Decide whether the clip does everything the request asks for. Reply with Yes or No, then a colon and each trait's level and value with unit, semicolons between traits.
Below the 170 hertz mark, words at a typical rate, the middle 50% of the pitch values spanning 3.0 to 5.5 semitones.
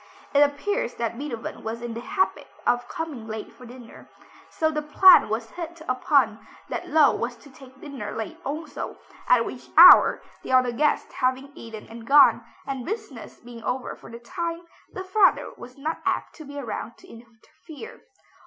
No: very high, 260 Hz; average, 175 wpm; average, 4.8 semitones